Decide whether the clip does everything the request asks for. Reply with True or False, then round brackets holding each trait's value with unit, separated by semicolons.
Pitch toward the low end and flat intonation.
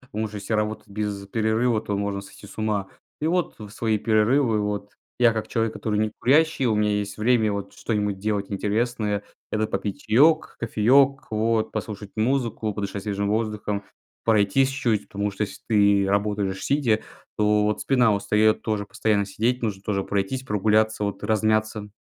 True (105 Hz; 1.8 semitones)